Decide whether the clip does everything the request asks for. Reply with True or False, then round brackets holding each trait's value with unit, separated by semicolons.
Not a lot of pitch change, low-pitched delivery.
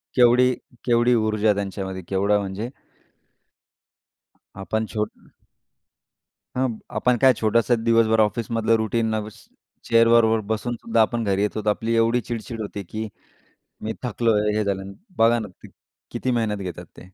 True (1.9 semitones; 110 Hz)